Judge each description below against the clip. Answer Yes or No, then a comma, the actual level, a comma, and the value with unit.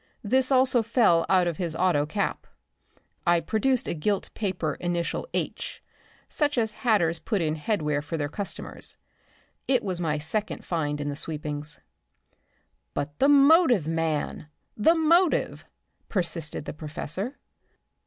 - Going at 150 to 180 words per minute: No, slow, 135 wpm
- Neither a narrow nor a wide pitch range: No, wide, 7.0 semitones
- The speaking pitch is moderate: Yes, medium, 175 Hz